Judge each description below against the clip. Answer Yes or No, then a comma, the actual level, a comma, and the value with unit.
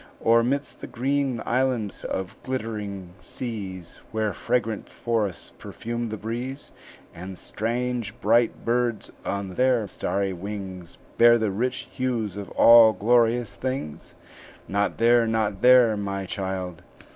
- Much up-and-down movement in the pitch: No, average, 3.5 semitones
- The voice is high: No, low, 110 Hz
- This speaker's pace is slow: Yes, slow, 125 wpm